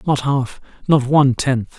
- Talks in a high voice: No, low, 135 Hz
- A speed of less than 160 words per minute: Yes, slow, 135 wpm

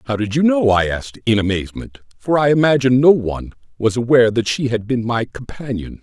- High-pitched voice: No, low, 120 Hz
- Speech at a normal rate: No, fast, 210 wpm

